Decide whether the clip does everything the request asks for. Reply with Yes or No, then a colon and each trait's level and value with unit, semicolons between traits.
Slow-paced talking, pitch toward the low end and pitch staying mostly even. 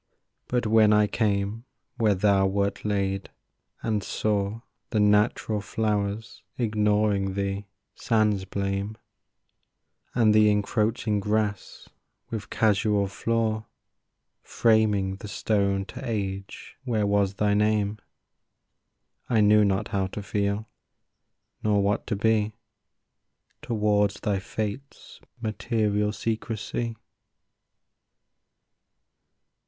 Yes: slow, 95 wpm; low, 105 Hz; narrow, 1.4 semitones